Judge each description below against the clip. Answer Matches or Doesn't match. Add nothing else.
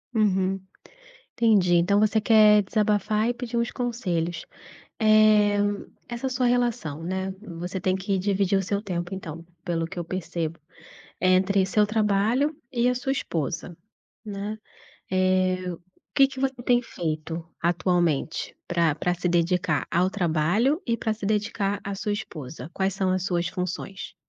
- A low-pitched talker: Doesn't match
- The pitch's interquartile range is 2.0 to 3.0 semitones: Doesn't match